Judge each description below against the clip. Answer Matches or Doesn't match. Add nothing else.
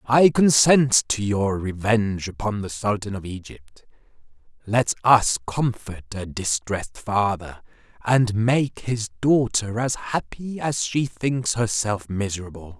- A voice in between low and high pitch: Doesn't match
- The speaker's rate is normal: Doesn't match